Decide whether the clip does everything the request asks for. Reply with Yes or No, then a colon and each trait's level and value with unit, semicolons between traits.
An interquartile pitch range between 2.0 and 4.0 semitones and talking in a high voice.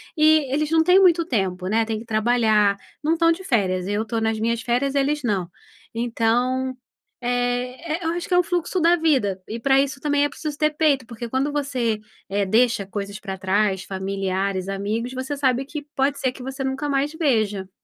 No: wide, 5.5 semitones; very high, 250 Hz